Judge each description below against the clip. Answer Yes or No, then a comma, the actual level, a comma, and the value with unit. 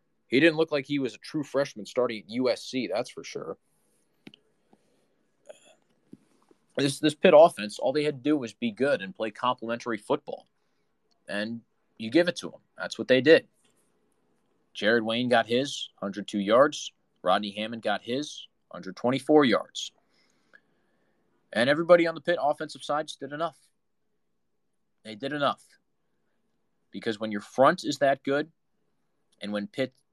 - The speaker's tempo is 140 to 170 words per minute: Yes, average, 150 wpm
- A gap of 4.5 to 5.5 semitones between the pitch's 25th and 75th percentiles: Yes, average, 5.2 semitones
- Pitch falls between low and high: No, low, 130 Hz